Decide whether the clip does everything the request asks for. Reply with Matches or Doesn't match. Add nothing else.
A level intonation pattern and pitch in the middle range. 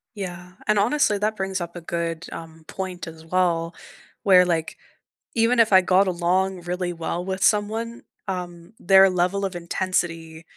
Matches